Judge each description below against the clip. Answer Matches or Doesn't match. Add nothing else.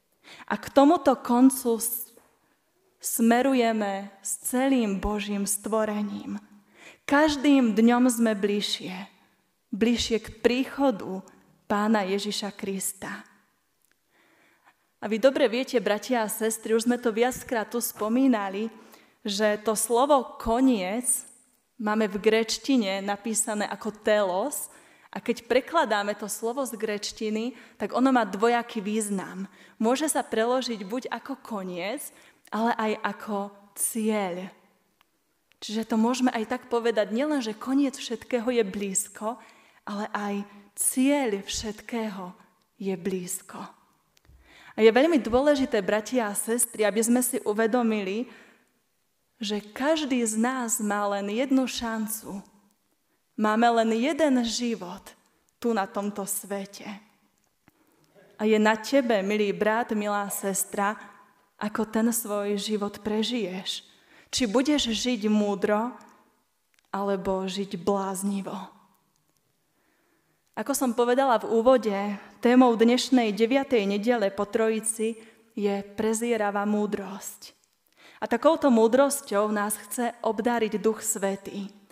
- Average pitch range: Matches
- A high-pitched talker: Matches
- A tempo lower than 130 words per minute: Matches